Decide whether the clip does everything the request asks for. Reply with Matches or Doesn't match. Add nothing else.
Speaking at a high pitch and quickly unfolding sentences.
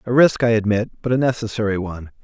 Doesn't match